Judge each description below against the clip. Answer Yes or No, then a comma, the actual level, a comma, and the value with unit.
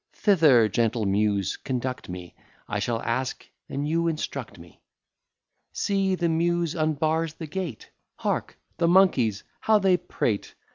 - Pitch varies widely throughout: Yes, wide, 7.2 semitones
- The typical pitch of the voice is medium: Yes, medium, 145 Hz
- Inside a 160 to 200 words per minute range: No, slow, 135 wpm